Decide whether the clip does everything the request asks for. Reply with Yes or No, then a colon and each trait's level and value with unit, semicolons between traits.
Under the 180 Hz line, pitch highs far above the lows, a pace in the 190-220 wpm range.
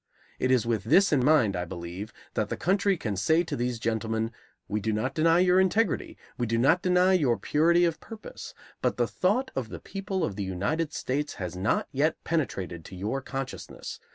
Yes: low, 135 Hz; wide, 8.0 semitones; average, 200 wpm